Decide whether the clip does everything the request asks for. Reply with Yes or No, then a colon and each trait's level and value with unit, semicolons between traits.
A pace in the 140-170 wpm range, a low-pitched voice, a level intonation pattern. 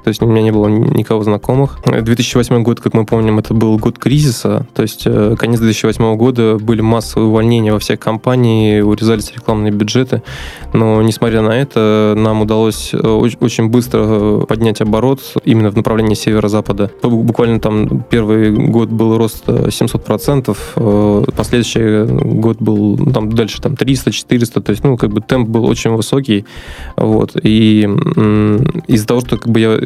Yes: average, 155 wpm; low, 110 Hz; narrow, 1.9 semitones